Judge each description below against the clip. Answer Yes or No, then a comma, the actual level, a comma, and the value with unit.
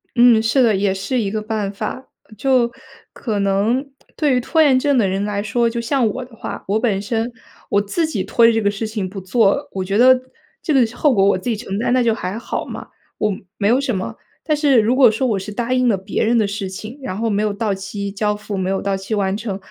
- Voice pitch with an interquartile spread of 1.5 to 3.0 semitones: No, average, 3.7 semitones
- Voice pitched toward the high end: Yes, high, 220 Hz